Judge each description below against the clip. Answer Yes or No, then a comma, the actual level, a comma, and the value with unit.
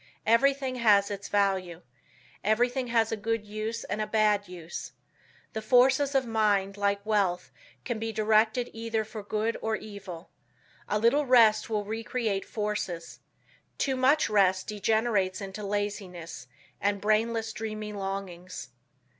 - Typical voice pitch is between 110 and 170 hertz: No, high, 215 Hz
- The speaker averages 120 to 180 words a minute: Yes, average, 140 wpm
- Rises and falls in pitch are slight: Yes, narrow, 2.2 semitones